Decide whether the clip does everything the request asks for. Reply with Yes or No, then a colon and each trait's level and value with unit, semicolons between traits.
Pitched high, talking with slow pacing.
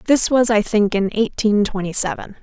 No: high, 215 Hz; average, 200 wpm